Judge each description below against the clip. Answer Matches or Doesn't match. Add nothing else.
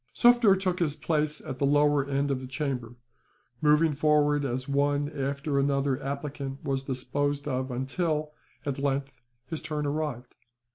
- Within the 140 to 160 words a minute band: Matches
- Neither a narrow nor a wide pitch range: Doesn't match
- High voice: Doesn't match